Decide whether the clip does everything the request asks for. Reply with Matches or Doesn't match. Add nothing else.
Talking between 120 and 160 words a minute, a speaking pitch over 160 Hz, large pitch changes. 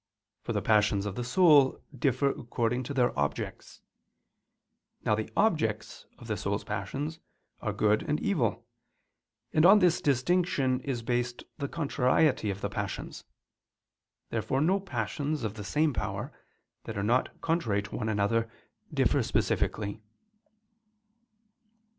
Doesn't match